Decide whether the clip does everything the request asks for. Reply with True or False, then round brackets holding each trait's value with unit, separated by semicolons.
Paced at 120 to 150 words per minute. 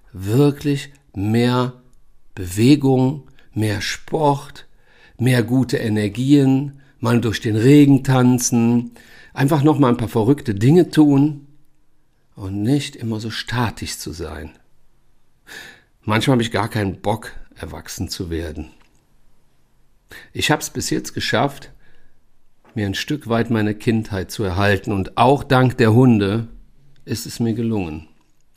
True (125 wpm)